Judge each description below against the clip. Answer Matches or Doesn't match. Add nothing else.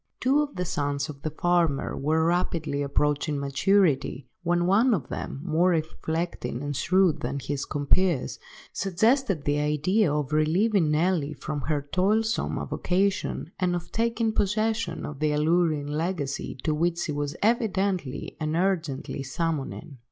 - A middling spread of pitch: Matches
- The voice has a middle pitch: Matches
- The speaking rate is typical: Matches